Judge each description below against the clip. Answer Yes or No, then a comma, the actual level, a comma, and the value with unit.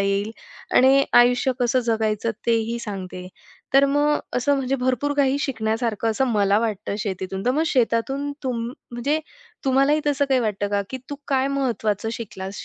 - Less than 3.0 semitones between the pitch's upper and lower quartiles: No, average, 4.2 semitones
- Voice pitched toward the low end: No, high, 240 Hz